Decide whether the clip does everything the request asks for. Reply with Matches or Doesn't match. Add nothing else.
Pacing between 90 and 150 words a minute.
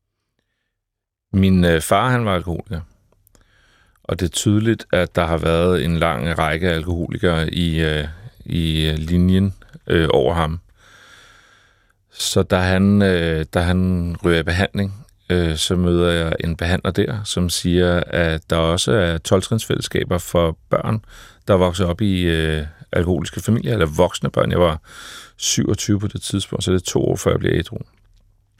Matches